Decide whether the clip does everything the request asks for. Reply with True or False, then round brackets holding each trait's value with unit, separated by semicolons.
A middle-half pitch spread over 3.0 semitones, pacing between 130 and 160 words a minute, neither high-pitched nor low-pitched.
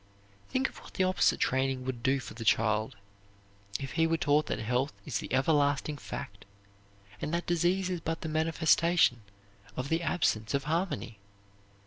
False (4.4 semitones; 170 wpm; 145 Hz)